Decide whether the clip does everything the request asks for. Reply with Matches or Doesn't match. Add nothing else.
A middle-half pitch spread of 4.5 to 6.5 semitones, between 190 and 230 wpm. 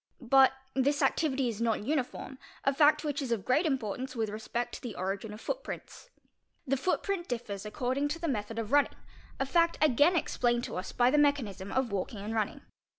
Matches